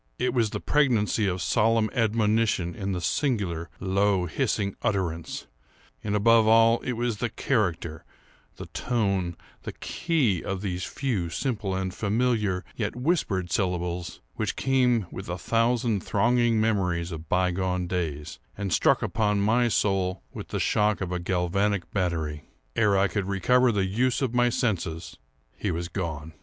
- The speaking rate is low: No, average, 150 wpm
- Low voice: Yes, low, 100 Hz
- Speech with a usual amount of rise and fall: Yes, average, 4.2 semitones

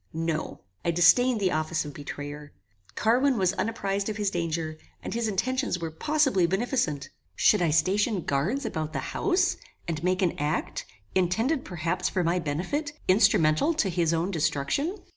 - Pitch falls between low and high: Yes, medium, 180 Hz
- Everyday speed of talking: Yes, average, 160 wpm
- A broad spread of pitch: Yes, wide, 6.0 semitones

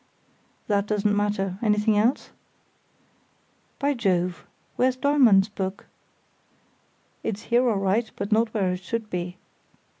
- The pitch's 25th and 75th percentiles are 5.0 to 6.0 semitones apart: No, average, 3.0 semitones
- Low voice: No, high, 210 Hz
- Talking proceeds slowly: Yes, slow, 115 wpm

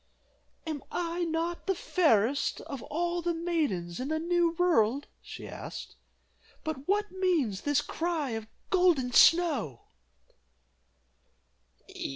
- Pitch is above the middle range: Yes, very high, 325 Hz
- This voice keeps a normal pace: No, slow, 115 wpm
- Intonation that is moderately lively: Yes, average, 4.7 semitones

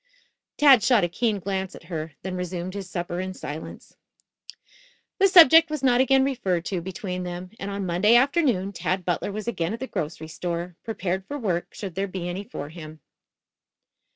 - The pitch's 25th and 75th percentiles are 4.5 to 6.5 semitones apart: Yes, average, 4.9 semitones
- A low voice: No, high, 190 Hz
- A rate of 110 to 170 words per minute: No, average, 180 wpm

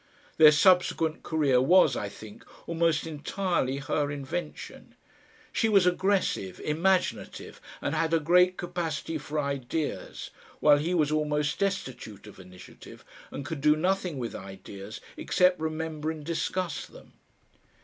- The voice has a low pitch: No, medium, 155 Hz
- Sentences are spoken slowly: Yes, slow, 130 wpm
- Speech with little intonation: No, average, 3.9 semitones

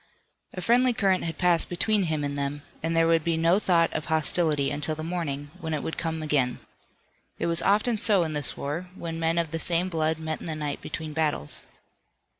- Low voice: No, medium, 165 Hz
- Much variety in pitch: No, narrow, 2.4 semitones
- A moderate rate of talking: No, fast, 215 wpm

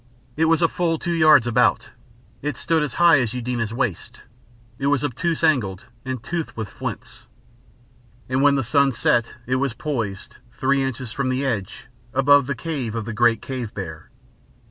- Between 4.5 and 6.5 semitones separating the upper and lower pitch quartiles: No, average, 4.0 semitones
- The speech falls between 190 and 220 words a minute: No, average, 170 wpm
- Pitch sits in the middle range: No, low, 130 Hz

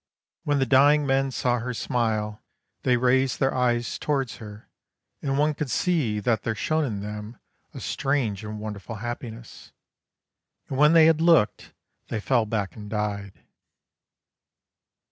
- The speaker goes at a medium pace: Yes, average, 145 wpm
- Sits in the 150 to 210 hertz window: No, low, 120 Hz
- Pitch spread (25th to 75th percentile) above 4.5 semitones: No, average, 4.2 semitones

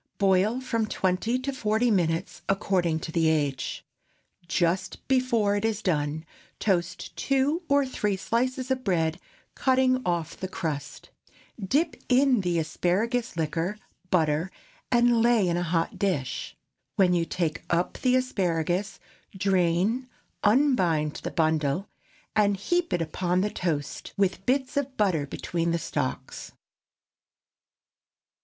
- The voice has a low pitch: No, high, 190 Hz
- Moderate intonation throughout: No, wide, 6.2 semitones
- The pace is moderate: No, slow, 130 wpm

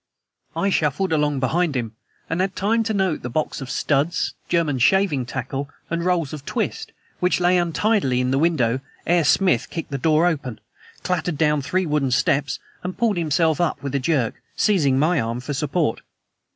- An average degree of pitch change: Yes, average, 4.7 semitones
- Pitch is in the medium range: Yes, medium, 155 Hz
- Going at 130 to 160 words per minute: No, average, 180 wpm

